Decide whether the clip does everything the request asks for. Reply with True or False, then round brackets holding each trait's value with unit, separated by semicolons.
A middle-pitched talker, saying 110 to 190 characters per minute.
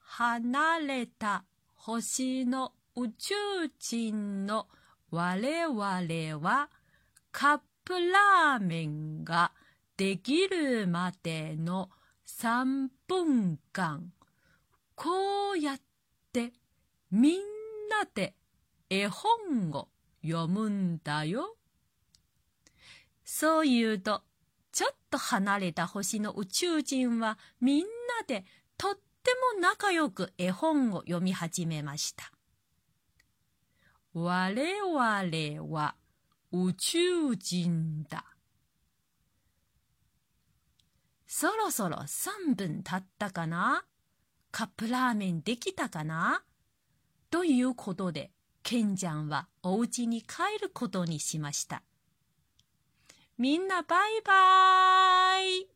False (230 Hz; 155 characters per minute)